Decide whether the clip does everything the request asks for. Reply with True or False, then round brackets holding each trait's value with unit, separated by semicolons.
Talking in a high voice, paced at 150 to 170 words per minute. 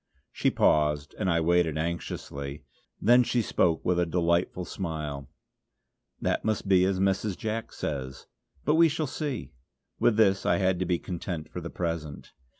False (90 Hz; 160 wpm)